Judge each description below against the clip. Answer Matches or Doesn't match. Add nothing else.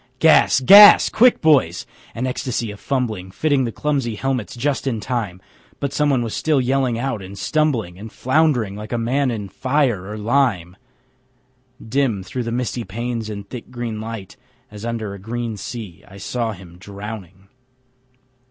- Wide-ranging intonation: Doesn't match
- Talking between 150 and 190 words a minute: Matches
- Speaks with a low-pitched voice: Matches